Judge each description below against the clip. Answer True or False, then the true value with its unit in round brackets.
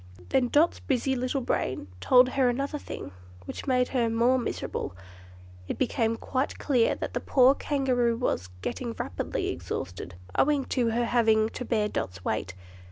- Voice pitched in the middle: False (245 Hz)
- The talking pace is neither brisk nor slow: True (160 wpm)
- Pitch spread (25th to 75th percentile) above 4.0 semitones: False (2.6 semitones)